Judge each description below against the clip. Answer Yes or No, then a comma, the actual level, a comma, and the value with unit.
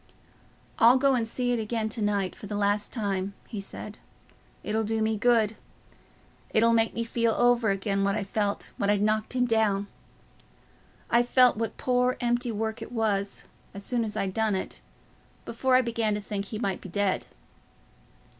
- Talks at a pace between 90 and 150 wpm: No, average, 180 wpm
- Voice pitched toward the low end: No, high, 220 Hz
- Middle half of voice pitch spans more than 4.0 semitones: No, narrow, 2.5 semitones